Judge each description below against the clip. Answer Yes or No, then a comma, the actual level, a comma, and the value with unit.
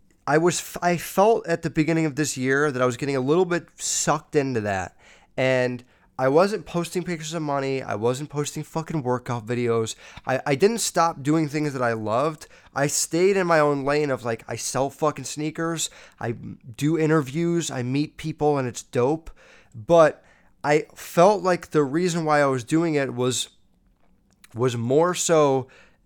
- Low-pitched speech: No, medium, 150 Hz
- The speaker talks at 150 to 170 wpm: No, average, 180 wpm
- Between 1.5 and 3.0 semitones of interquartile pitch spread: No, average, 4.3 semitones